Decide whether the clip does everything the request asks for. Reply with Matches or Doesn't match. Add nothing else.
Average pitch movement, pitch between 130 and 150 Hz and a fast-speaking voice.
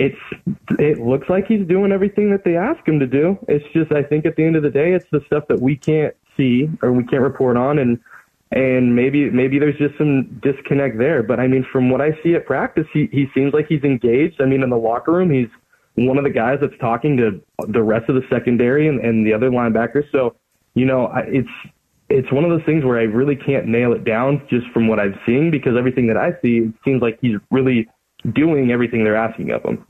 Matches